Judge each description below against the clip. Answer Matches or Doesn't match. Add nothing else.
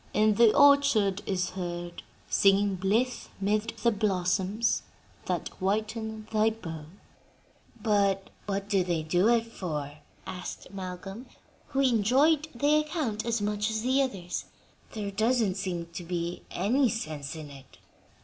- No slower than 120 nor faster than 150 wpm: Matches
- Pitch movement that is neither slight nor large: Matches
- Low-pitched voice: Doesn't match